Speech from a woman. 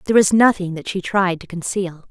Yes: female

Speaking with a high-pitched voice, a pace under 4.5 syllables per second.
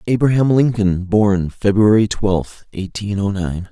No: low, 100 Hz; 4.0 syllables/s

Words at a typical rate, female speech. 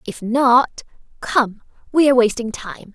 No: slow, 120 wpm; female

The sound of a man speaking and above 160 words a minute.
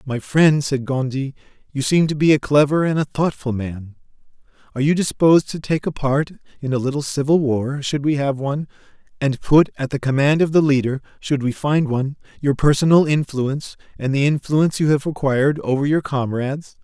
Yes: male; average, 190 wpm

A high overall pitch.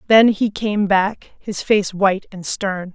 Yes: high, 200 Hz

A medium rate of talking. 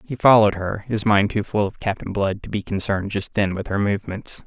No: fast, 240 wpm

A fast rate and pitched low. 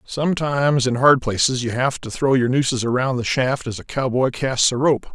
Yes: fast, 220 wpm; low, 130 Hz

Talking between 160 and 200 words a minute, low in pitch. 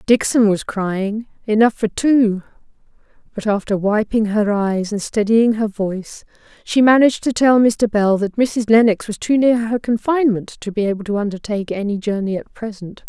No: average, 170 wpm; high, 215 Hz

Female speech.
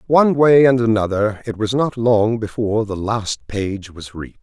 No: male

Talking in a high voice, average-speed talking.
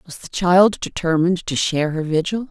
No: medium, 170 Hz; average, 190 wpm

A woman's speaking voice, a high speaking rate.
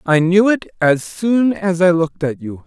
No: male; fast, 225 wpm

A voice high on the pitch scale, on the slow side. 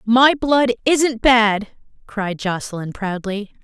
Yes: high, 225 Hz; slow, 115 wpm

